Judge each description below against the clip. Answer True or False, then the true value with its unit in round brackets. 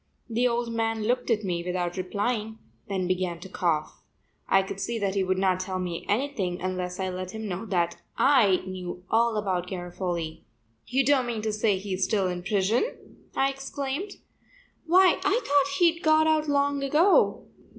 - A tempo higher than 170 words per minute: True (180 wpm)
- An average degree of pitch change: False (6.2 semitones)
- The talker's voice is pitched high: True (205 Hz)